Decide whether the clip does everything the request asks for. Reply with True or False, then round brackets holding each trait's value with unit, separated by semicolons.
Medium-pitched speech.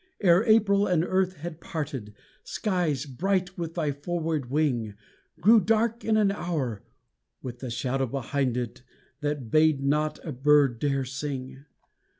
True (150 Hz)